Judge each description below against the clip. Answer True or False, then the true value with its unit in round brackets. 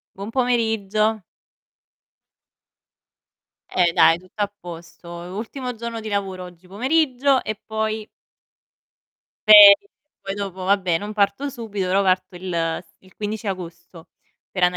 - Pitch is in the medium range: False (200 Hz)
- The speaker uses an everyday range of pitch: True (3.1 semitones)